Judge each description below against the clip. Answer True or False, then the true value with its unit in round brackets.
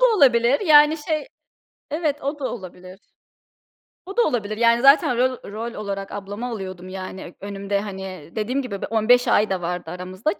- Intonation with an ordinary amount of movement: False (6.2 semitones)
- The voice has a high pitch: True (220 Hz)